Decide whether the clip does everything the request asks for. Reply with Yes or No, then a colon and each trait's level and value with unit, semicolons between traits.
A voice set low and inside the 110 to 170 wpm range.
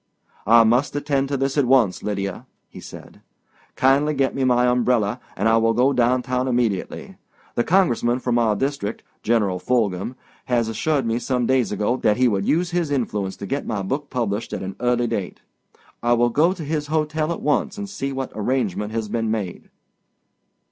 No: low, 125 Hz; average, 185 wpm